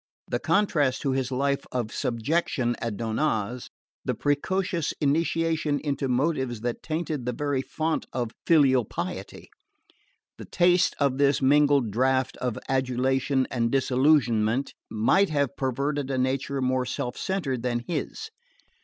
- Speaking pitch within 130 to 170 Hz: Yes, low, 135 Hz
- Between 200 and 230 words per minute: No, slow, 135 wpm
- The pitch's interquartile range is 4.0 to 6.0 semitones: No, average, 3.0 semitones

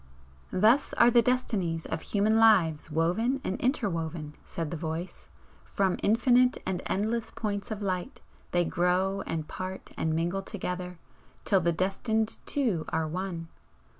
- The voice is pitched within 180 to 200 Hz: Yes, high, 190 Hz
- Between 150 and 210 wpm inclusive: No, average, 140 wpm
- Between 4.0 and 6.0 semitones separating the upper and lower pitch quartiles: Yes, average, 4.8 semitones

